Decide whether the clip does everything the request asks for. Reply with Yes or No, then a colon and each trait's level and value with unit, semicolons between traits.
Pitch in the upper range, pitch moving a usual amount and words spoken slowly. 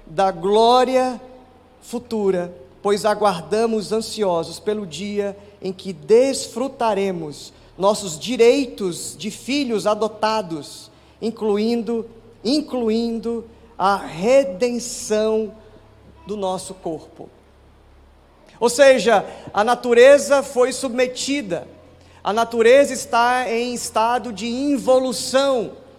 Yes: high, 220 Hz; average, 4.4 semitones; slow, 85 wpm